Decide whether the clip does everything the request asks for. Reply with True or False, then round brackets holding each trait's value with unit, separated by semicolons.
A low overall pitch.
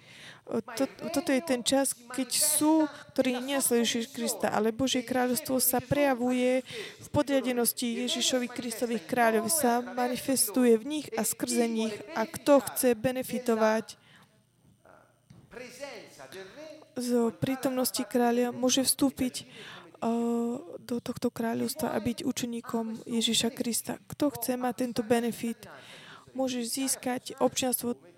False (245 Hz)